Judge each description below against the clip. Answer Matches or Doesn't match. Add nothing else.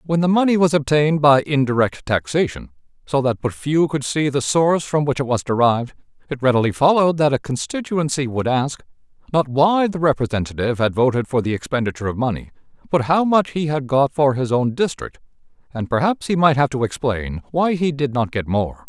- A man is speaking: Matches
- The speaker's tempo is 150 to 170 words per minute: Doesn't match